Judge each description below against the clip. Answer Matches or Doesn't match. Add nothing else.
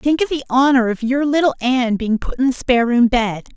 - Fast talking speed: Matches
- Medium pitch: Doesn't match